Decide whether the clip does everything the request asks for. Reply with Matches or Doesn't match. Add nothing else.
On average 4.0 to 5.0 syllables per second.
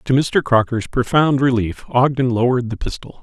Doesn't match